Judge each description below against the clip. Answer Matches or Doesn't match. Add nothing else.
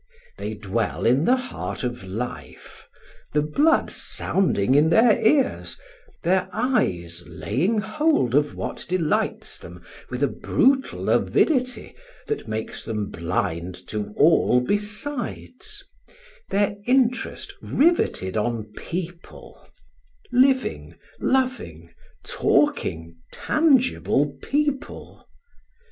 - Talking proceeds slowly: Matches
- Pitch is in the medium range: Matches